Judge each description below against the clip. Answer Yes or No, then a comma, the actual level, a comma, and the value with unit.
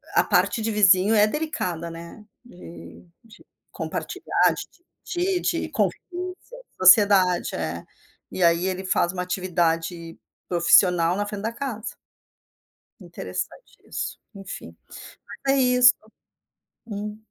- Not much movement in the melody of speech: No, average, 4.7 semitones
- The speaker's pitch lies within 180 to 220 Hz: Yes, high, 190 Hz